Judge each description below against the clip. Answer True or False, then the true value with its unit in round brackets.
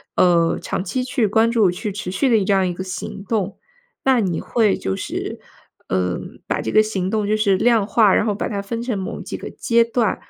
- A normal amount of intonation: True (3.4 semitones)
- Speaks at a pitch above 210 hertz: False (205 Hz)